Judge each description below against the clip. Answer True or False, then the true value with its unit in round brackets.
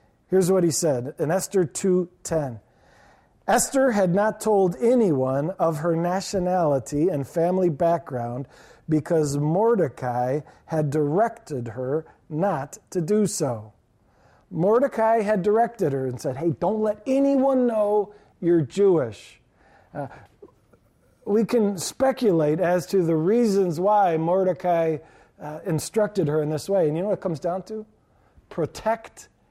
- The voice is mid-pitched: True (180 Hz)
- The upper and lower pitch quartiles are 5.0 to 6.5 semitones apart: True (5.3 semitones)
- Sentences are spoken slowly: True (130 wpm)